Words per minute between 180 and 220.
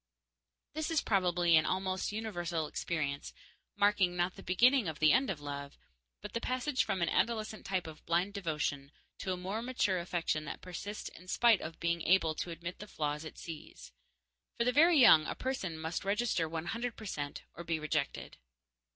Yes: average, 185 wpm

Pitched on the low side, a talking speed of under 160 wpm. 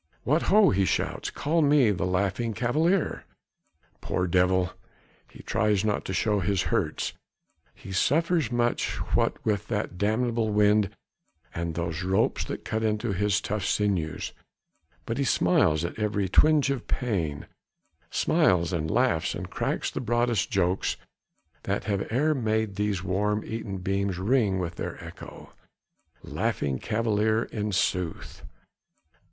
Yes: low, 105 Hz; average, 140 wpm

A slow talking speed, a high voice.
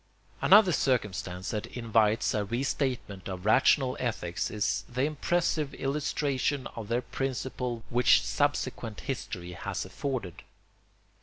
No: slow, 110 wpm; low, 125 Hz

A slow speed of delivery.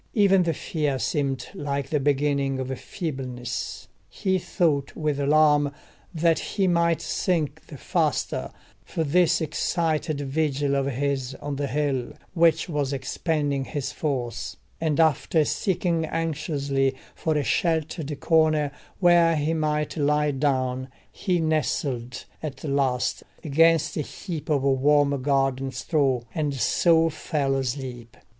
Yes: slow, 130 wpm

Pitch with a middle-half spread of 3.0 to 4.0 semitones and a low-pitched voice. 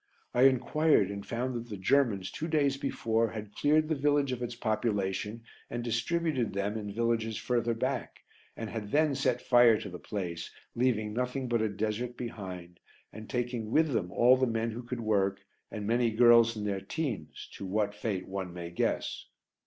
Yes: average, 3.4 semitones; low, 115 Hz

